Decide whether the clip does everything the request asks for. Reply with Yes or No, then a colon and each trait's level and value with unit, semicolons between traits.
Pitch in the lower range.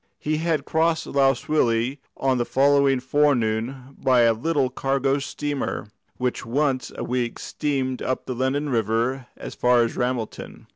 Yes: low, 130 Hz